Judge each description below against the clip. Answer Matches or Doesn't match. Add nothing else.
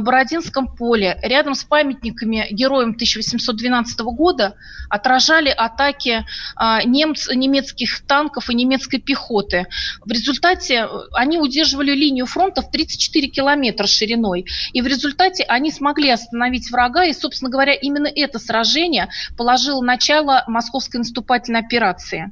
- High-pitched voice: Matches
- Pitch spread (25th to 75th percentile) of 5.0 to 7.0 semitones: Doesn't match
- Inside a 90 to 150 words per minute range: Matches